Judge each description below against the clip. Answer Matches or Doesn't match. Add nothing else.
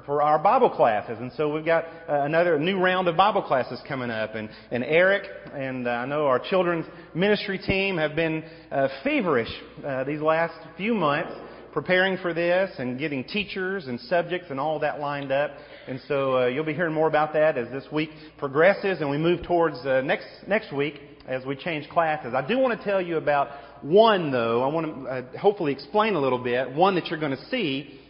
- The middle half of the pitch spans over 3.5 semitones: Matches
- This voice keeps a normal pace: Doesn't match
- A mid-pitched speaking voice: Matches